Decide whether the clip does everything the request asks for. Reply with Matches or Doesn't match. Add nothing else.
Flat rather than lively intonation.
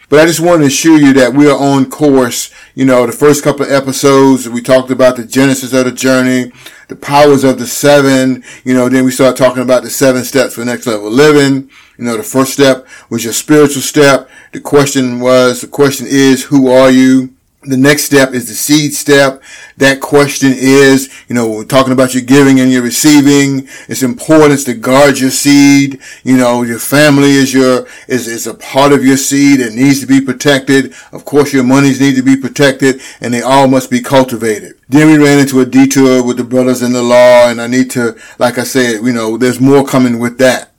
Matches